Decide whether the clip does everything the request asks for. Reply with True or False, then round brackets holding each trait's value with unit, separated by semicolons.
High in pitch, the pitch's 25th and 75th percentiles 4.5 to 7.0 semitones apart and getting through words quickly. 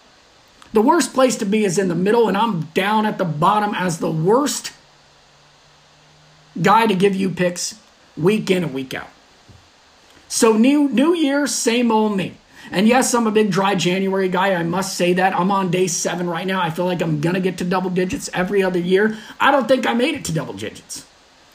False (195 Hz; 3.8 semitones; 210 wpm)